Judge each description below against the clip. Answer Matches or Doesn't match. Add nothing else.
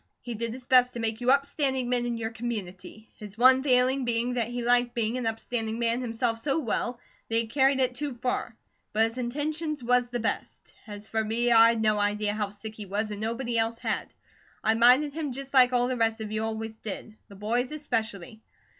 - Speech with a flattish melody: Matches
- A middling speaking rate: Doesn't match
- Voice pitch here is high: Matches